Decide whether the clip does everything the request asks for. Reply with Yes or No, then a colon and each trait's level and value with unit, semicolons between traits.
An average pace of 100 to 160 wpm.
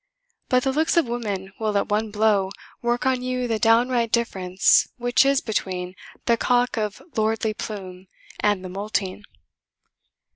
Yes: average, 150 wpm